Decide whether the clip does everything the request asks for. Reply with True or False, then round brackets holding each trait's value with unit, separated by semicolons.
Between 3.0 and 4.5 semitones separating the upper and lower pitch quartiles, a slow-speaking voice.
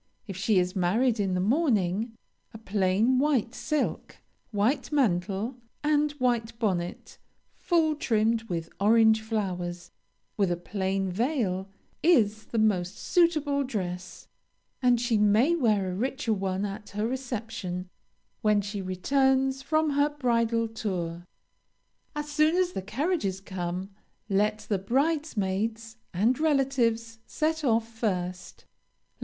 False (5.5 semitones; 125 wpm)